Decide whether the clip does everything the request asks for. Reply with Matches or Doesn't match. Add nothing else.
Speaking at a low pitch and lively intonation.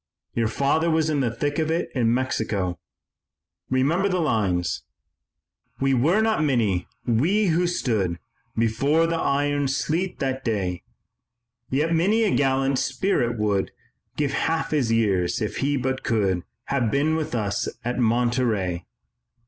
Matches